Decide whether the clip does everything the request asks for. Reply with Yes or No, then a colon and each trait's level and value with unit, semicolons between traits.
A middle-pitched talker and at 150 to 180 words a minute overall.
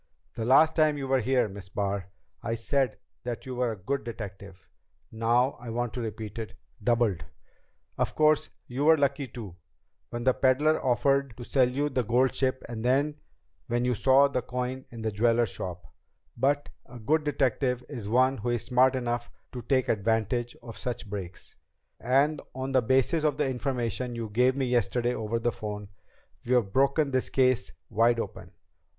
No: low, 125 Hz; average, 175 wpm